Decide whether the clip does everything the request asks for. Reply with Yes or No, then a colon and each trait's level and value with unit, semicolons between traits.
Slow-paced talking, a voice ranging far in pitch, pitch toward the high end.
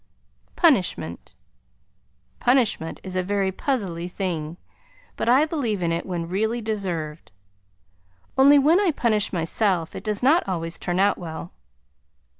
Yes: slow, 130 wpm; wide, 6.1 semitones; high, 195 Hz